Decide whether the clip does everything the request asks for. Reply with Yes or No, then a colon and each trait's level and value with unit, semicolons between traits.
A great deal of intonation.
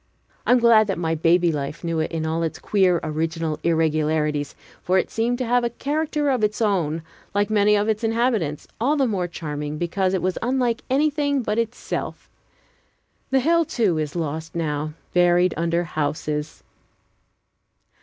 Yes: wide, 6.5 semitones